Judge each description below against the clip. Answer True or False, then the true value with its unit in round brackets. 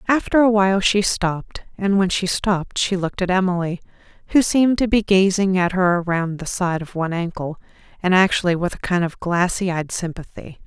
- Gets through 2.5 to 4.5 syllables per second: False (5.5 syllables/s)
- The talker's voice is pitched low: False (185 Hz)